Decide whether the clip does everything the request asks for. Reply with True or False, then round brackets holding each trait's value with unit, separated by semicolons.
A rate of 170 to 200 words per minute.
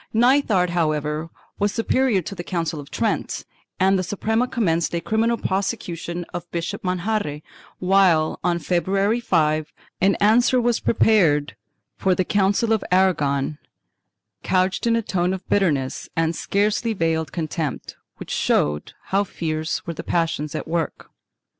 False (140 wpm)